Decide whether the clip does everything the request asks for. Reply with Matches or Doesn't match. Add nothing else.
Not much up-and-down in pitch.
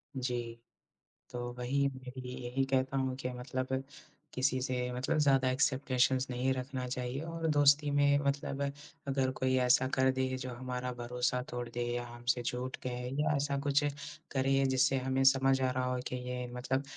Matches